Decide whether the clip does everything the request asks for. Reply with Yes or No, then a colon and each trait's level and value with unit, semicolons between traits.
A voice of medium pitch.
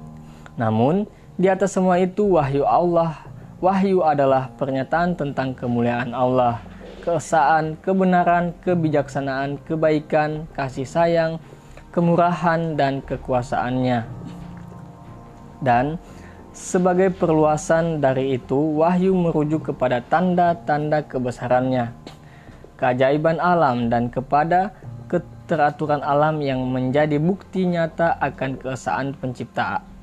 Yes: medium, 145 Hz